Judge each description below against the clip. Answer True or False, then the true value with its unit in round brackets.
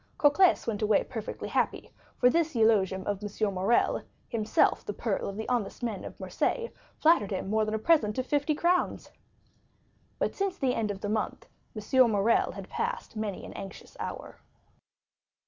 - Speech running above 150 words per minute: True (170 wpm)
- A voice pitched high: True (220 Hz)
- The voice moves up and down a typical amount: True (4.3 semitones)